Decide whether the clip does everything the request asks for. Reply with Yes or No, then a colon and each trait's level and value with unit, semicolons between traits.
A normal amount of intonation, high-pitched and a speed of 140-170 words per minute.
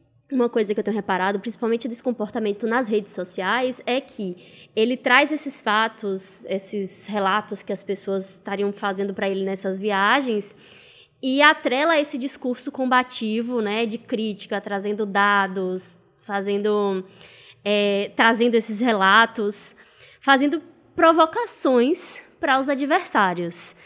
No: average, 4.2 semitones; high, 215 Hz; average, 125 wpm